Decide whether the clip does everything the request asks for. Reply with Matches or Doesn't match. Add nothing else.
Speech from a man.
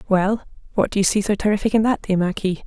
Doesn't match